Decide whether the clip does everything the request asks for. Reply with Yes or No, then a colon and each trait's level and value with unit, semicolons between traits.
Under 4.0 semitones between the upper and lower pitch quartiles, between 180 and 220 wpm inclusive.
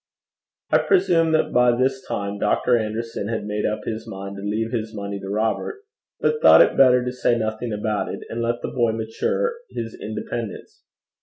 Yes: narrow, 2.6 semitones; average, 185 wpm